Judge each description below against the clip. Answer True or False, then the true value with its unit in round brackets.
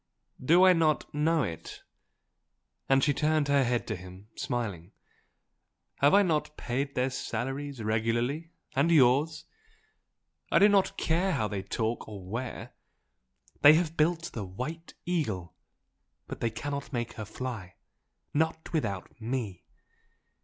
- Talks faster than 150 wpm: False (135 wpm)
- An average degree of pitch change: False (6.0 semitones)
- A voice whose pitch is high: False (135 Hz)